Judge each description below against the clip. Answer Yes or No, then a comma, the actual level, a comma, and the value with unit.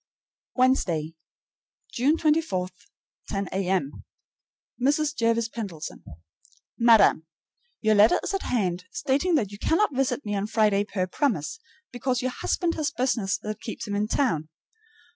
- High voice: Yes, high, 225 Hz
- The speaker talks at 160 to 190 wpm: No, slow, 135 wpm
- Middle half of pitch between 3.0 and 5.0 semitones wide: No, wide, 5.6 semitones